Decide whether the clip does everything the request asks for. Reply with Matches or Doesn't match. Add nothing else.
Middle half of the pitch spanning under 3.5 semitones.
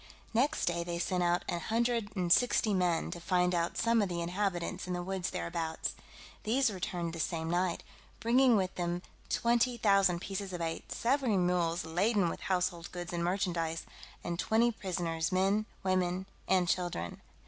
Matches